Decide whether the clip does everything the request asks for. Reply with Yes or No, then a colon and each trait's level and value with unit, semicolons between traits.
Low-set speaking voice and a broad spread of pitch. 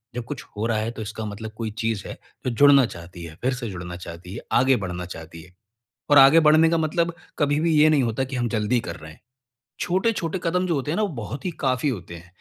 Yes: low, 120 Hz; wide, 8.0 semitones